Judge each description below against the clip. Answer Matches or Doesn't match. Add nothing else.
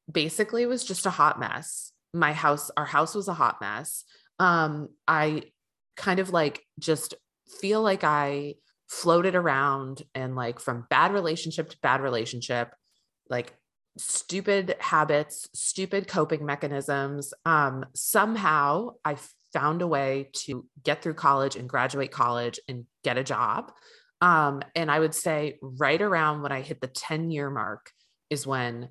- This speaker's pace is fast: Doesn't match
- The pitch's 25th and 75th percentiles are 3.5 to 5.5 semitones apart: Matches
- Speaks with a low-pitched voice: Doesn't match